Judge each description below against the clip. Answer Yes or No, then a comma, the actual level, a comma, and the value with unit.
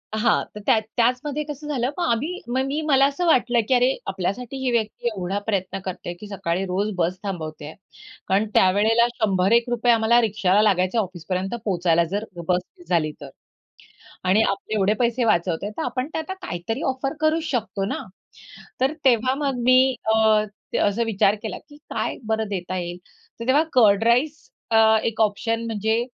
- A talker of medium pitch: No, high, 220 Hz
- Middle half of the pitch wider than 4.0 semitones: Yes, average, 4.6 semitones